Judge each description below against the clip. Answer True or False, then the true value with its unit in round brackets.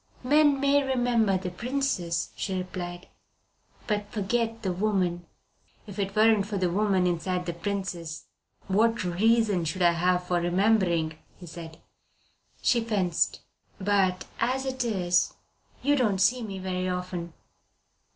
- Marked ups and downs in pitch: False (4.1 semitones)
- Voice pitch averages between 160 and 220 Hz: True (190 Hz)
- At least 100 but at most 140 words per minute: True (135 wpm)